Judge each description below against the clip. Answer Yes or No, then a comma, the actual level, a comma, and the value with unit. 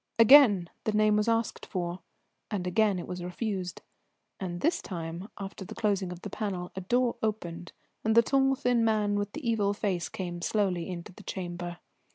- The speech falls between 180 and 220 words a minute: Yes, average, 185 wpm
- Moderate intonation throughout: Yes, average, 3.6 semitones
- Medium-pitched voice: No, high, 200 Hz